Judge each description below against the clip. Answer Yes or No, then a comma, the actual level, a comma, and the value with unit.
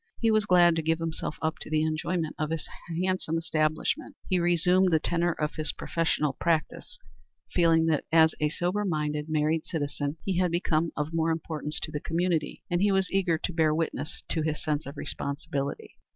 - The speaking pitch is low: No, medium, 160 Hz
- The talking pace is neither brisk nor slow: Yes, average, 190 wpm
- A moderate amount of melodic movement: No, narrow, 2.2 semitones